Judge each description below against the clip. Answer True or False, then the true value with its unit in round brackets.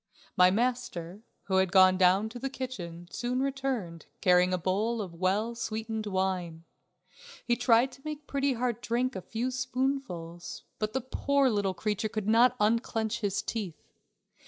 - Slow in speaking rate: False (155 wpm)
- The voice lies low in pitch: False (220 Hz)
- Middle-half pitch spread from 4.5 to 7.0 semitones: True (5.0 semitones)